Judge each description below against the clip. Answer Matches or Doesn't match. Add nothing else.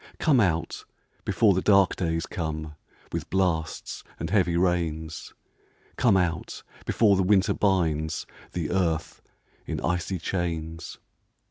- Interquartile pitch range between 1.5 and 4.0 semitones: Matches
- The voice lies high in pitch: Doesn't match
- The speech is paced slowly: Matches